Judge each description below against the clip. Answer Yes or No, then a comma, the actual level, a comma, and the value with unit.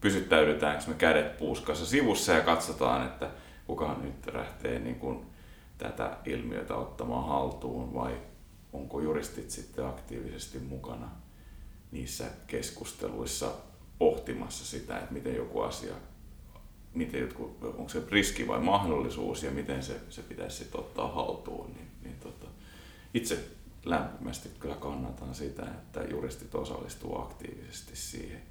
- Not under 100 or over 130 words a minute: Yes, average, 120 wpm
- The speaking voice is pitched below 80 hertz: Yes, very low, 70 Hz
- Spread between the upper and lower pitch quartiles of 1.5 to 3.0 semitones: Yes, narrow, 2.4 semitones